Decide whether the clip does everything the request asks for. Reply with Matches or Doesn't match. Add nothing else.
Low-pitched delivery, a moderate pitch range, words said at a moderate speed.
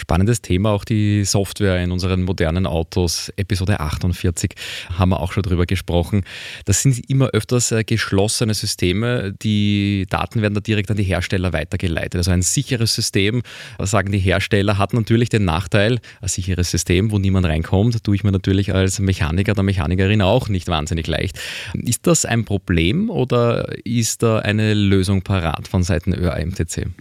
Matches